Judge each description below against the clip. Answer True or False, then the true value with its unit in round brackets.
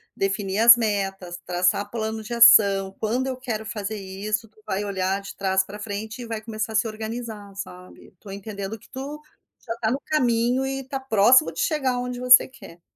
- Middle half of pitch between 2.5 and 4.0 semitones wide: True (3.4 semitones)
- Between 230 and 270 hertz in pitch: False (220 Hz)